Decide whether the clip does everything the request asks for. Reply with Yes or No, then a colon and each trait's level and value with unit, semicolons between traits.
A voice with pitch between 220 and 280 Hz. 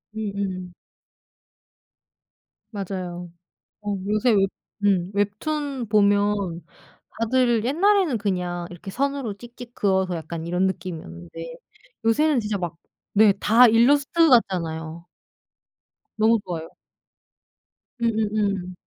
No: high, 205 Hz